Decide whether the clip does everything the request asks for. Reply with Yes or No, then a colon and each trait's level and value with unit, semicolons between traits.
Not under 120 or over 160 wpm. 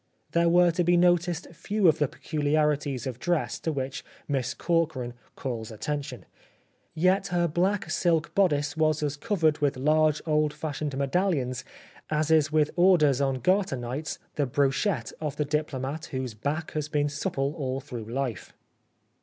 Yes: average, 155 wpm